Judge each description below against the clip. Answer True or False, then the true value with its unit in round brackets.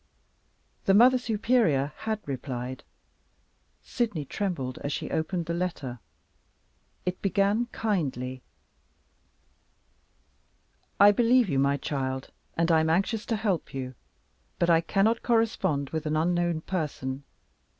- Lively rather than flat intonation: True (6.8 semitones)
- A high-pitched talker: False (170 Hz)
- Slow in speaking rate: True (120 wpm)